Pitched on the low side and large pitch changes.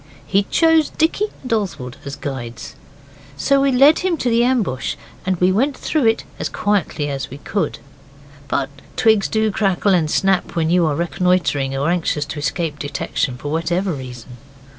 No: medium, 180 Hz; wide, 7.5 semitones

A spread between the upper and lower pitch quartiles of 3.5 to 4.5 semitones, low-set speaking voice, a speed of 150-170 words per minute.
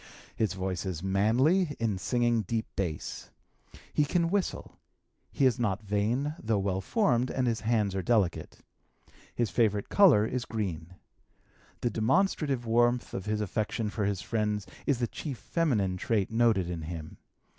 Yes: average, 4.0 semitones; low, 110 Hz; average, 155 wpm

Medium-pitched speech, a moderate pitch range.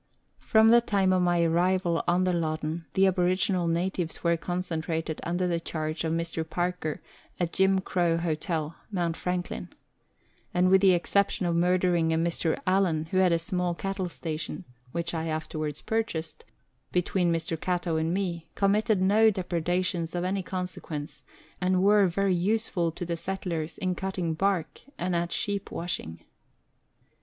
No: medium, 175 Hz; narrow, 2.1 semitones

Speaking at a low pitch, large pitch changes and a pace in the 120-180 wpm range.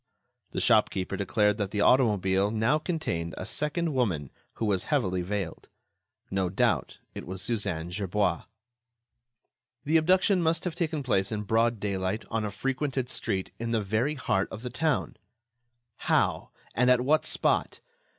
Yes: low, 110 Hz; wide, 5.8 semitones; average, 150 wpm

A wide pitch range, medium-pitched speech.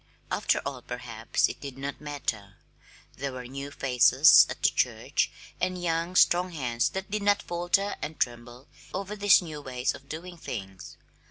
Yes: wide, 5.9 semitones; medium, 145 Hz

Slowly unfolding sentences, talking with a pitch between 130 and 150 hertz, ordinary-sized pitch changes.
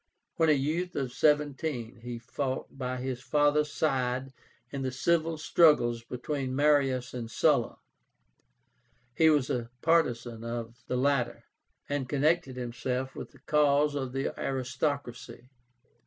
Yes: slow, 130 wpm; low, 135 Hz; average, 3.0 semitones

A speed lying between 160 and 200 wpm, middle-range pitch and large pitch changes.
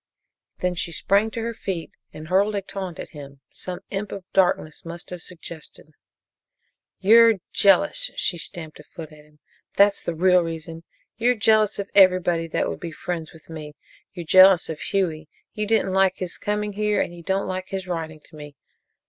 No: average, 185 wpm; medium, 180 Hz; average, 3.5 semitones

